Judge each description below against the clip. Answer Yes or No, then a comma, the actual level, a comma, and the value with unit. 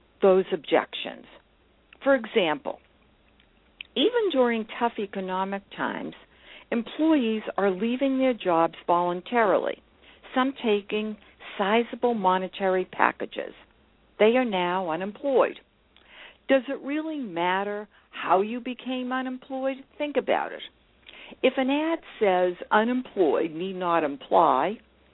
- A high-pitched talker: Yes, high, 225 Hz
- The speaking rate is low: Yes, slow, 105 wpm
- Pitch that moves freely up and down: Yes, wide, 5.7 semitones